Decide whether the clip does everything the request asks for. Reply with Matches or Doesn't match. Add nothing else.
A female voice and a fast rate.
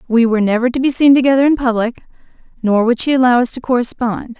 Matches